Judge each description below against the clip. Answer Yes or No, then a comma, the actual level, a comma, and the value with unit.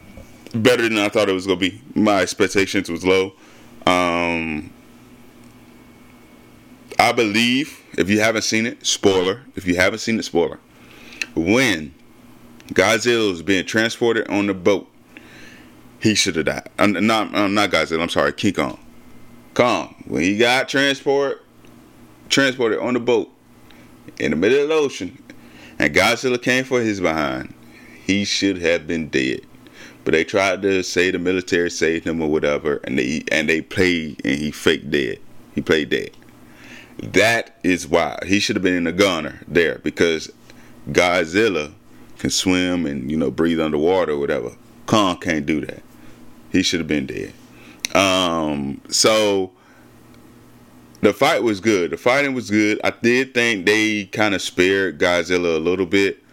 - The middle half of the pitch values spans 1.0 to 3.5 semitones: No, average, 4.3 semitones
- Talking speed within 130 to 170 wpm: Yes, average, 160 wpm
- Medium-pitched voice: No, very low, 95 Hz